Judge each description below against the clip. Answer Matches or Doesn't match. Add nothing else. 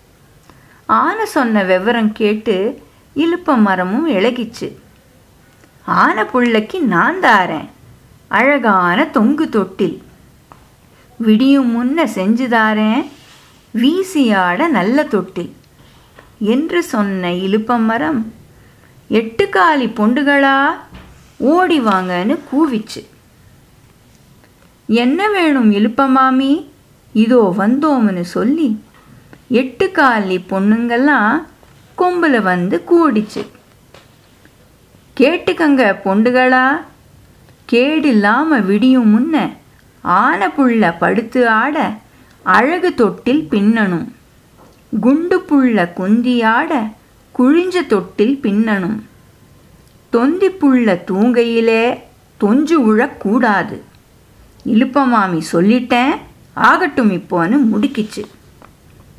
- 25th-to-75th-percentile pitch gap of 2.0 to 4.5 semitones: Doesn't match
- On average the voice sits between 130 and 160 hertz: Doesn't match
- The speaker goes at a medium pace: Doesn't match